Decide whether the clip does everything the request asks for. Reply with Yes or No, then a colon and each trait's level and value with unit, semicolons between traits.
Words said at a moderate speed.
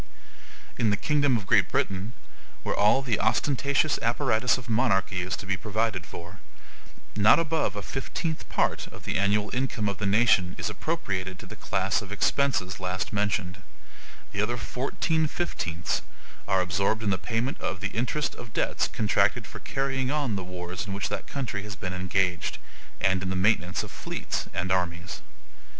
Yes: average, 170 wpm